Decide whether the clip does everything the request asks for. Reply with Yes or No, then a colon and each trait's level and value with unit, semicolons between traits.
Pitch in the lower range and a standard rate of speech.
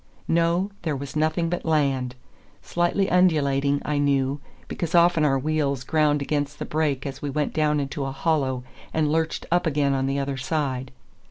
No: medium, 145 Hz; average, 170 wpm